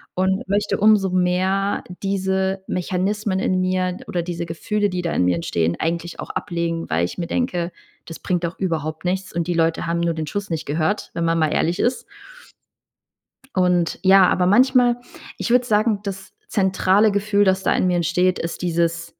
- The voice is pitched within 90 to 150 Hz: No, medium, 185 Hz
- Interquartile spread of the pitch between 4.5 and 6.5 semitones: No, narrow, 2.6 semitones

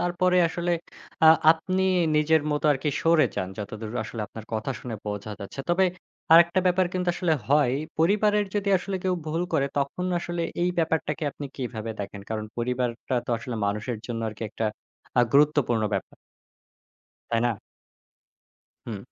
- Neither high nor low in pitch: Yes, medium, 150 Hz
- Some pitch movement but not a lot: No, wide, 7.0 semitones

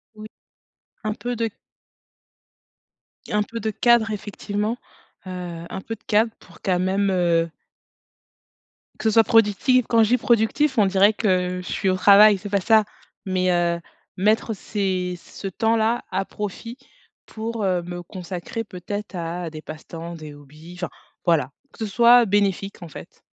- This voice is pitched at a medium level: No, high, 200 Hz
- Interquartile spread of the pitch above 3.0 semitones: Yes, average, 3.7 semitones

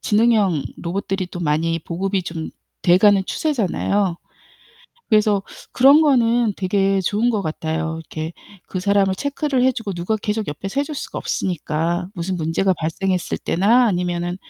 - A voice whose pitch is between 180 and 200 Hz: Yes, high, 195 Hz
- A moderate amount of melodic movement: Yes, average, 4.0 semitones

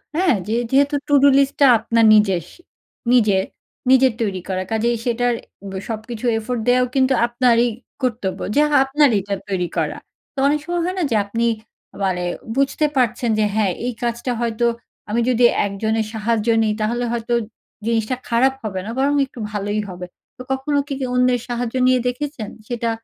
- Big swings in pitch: No, average, 3.3 semitones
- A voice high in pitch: Yes, high, 235 Hz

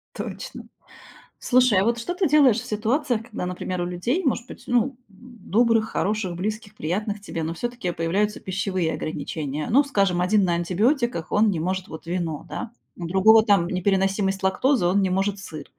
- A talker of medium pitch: No, high, 200 Hz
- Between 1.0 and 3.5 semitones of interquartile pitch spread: No, average, 4.5 semitones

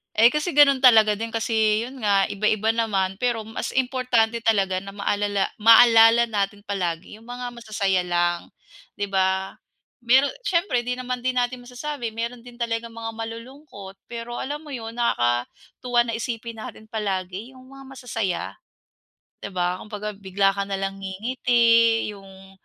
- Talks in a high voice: Yes, high, 225 Hz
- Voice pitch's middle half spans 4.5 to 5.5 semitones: No, average, 3.5 semitones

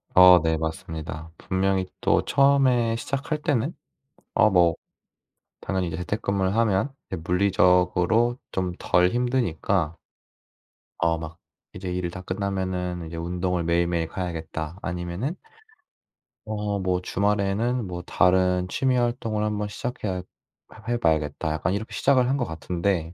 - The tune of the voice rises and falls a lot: No, average, 3.8 semitones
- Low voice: Yes, very low, 95 Hz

